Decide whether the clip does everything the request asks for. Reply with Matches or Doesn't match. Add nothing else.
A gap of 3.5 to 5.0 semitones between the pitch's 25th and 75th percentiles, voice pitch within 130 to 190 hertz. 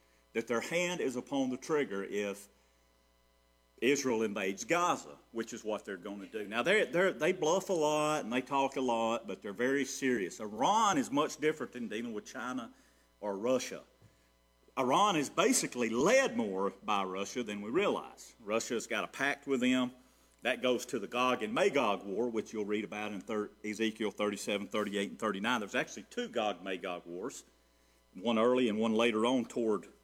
Doesn't match